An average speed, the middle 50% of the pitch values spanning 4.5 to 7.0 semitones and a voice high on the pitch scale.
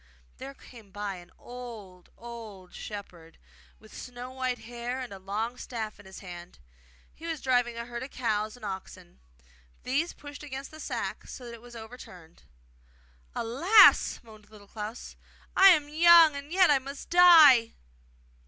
Yes: average, 160 wpm; average, 4.8 semitones; high, 240 Hz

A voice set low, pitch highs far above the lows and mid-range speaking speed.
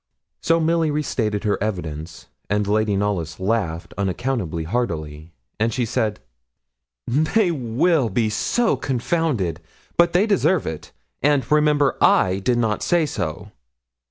No: low, 115 Hz; wide, 7.8 semitones; slow, 130 wpm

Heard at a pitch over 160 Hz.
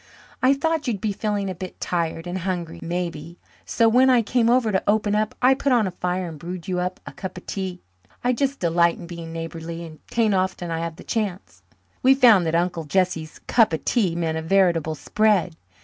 Yes: medium, 185 Hz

